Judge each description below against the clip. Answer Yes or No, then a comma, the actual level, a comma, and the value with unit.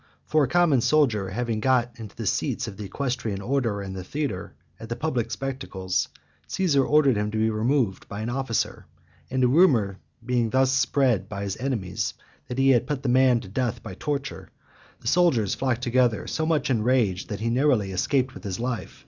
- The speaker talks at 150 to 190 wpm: No, average, 200 wpm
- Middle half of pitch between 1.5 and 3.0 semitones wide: No, average, 4.2 semitones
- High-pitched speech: No, low, 120 Hz